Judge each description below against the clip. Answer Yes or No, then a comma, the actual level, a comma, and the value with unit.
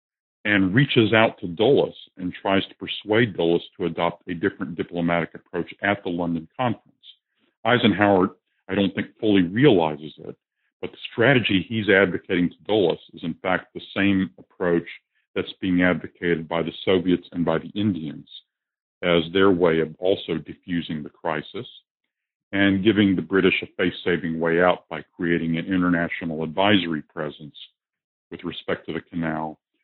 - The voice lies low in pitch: Yes, very low, 90 Hz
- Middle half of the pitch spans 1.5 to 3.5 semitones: Yes, average, 2.8 semitones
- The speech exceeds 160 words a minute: No, average, 155 wpm